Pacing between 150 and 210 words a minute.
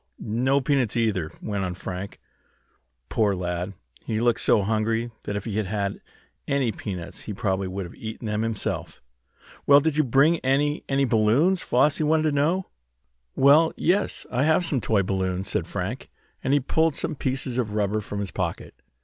Yes: average, 175 wpm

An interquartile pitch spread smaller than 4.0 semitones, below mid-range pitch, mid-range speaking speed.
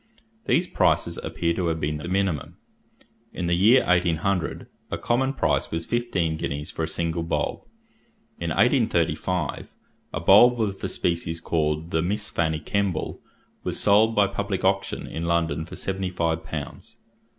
Yes: average, 3.6 semitones; very low, 85 Hz; average, 155 wpm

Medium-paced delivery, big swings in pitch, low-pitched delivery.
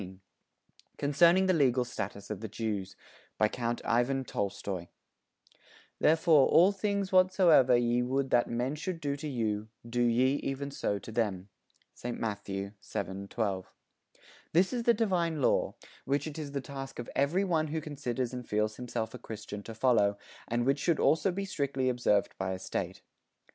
Yes: average, 170 wpm; wide, 6.0 semitones; low, 125 Hz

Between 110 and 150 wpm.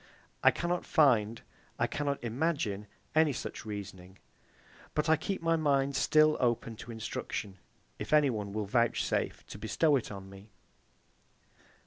Yes: average, 140 wpm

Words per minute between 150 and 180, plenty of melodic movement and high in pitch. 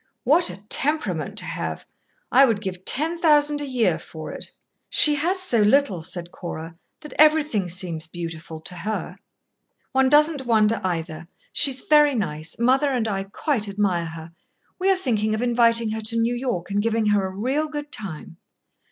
Yes: average, 175 wpm; wide, 7.7 semitones; high, 225 Hz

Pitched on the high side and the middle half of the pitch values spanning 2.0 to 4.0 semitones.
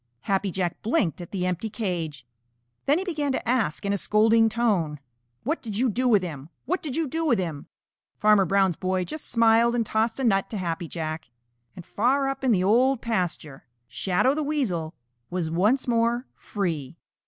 No: high, 210 Hz; wide, 5.6 semitones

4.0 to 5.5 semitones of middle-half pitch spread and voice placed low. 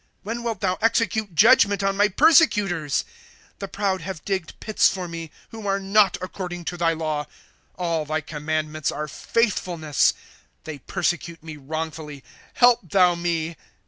No: average, 4.3 semitones; medium, 175 Hz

